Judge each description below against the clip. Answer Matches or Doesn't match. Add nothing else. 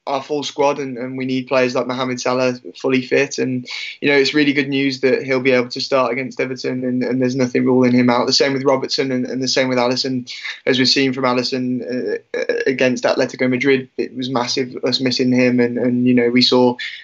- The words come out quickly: Matches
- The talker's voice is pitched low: Matches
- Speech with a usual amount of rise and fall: Doesn't match